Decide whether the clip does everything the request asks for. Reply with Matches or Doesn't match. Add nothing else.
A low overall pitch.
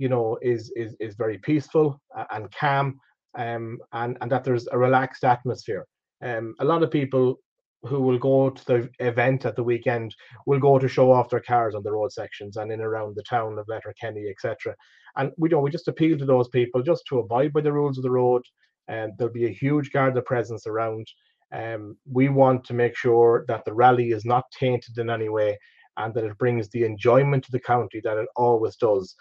Matches